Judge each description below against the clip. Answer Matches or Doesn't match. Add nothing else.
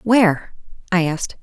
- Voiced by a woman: Matches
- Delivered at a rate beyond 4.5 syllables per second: Matches